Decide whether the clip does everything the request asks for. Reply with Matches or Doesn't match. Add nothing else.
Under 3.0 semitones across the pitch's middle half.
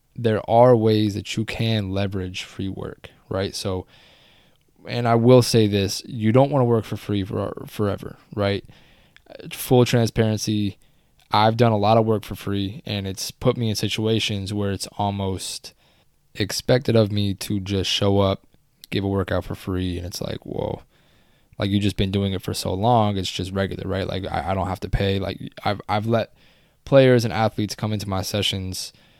Matches